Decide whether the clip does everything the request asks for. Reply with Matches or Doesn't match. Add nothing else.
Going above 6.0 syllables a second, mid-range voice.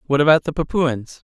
Doesn't match